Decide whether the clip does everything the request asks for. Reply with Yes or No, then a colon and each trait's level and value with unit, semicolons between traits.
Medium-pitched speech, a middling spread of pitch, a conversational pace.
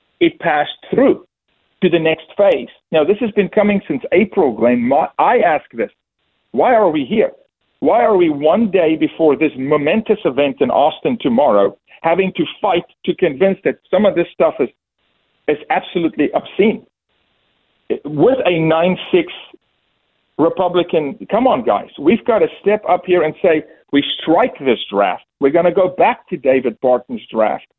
Yes: medium, 175 Hz; average, 4.5 semitones; average, 170 wpm